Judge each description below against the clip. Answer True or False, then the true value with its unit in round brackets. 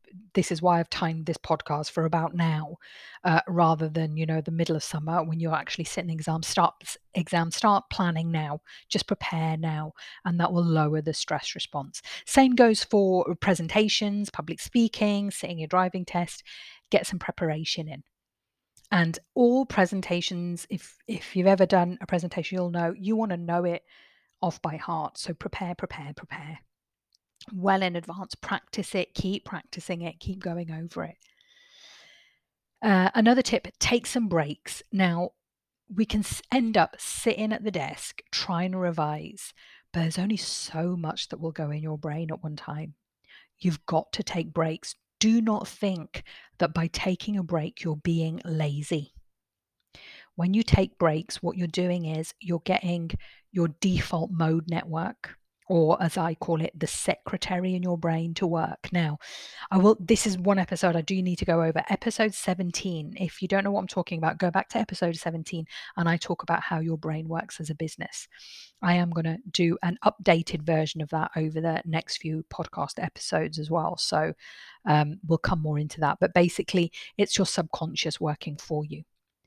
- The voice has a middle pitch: True (170 Hz)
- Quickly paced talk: False (175 wpm)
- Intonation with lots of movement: False (2.7 semitones)